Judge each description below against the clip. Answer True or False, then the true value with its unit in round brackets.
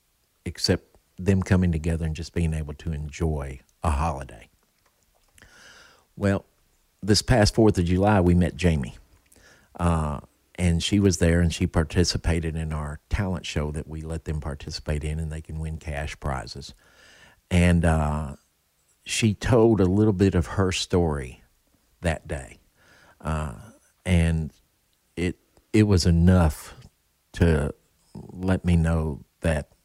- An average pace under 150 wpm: True (135 wpm)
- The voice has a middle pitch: False (85 Hz)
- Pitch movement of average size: True (3.1 semitones)